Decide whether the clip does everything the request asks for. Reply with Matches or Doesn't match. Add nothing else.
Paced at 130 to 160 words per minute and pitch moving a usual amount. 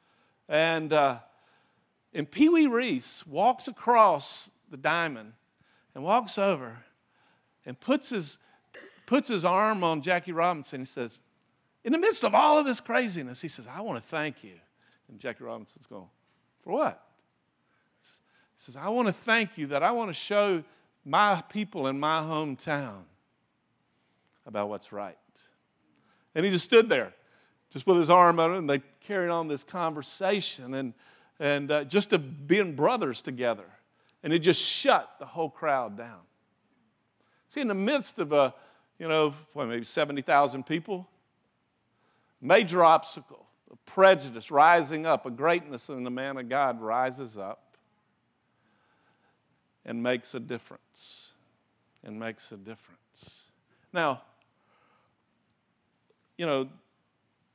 Doesn't match